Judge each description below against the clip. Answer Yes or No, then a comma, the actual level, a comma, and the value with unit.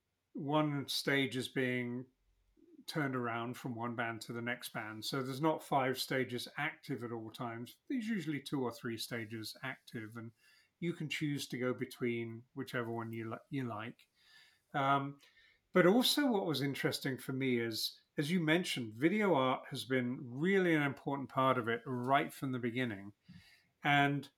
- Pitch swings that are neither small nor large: Yes, average, 3.6 semitones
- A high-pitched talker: No, low, 130 Hz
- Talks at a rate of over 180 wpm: No, average, 170 wpm